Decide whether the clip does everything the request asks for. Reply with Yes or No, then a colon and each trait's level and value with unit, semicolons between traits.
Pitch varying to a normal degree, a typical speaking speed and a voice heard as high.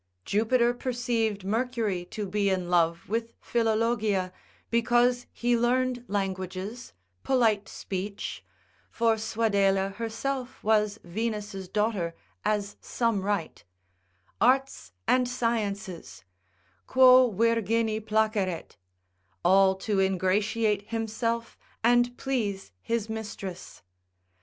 No: average, 3.2 semitones; slow, 95 wpm; high, 220 Hz